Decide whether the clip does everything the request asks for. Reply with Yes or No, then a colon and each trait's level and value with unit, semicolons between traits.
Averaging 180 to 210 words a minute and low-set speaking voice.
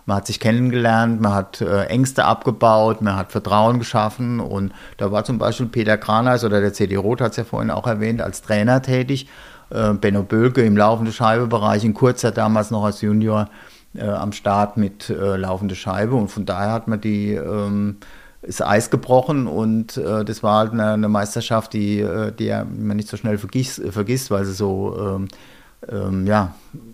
Yes: average, 185 wpm; low, 110 Hz